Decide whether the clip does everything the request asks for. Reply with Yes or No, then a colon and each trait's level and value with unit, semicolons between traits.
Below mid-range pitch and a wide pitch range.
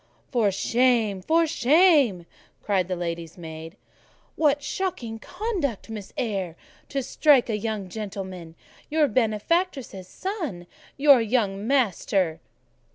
No: high, 225 Hz; wide, 7.0 semitones